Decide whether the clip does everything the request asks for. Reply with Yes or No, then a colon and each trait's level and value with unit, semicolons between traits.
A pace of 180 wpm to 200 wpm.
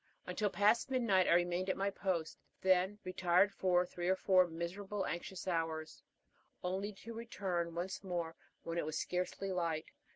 No: average, 160 wpm